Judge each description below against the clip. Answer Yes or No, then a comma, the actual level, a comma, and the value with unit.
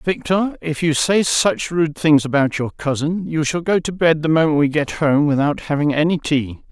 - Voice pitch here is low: No, medium, 155 Hz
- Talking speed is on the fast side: Yes, fast, 215 wpm